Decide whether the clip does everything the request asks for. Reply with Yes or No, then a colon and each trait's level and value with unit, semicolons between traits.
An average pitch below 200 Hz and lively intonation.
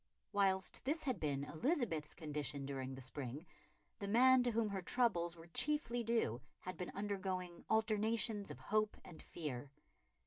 Yes: high, 190 Hz; wide, 6.9 semitones